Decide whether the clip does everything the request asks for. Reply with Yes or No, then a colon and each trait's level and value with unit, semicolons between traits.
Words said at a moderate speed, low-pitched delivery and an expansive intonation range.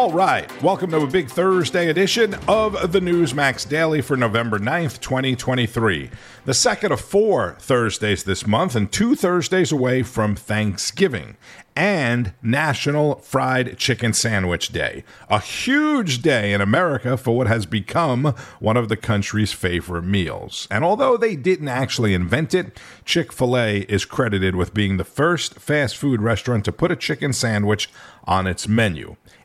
Yes: average, 155 wpm; low, 125 Hz; wide, 6.9 semitones